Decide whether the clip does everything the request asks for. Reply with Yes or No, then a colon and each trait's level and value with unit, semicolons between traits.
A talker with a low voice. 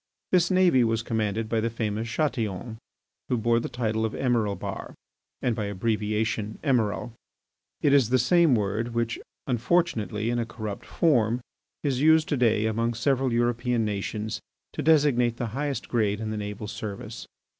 Yes: low, 115 Hz